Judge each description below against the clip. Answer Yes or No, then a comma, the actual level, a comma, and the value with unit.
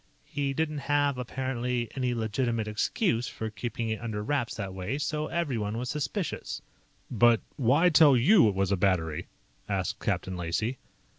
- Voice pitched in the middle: No, low, 120 Hz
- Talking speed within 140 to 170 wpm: Yes, average, 155 wpm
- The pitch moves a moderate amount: Yes, average, 4.9 semitones